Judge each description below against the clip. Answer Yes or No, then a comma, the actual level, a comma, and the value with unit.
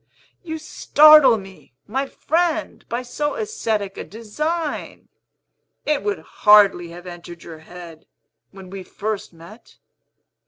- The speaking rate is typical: No, slow, 120 wpm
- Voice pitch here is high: Yes, high, 215 Hz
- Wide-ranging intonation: Yes, wide, 8.9 semitones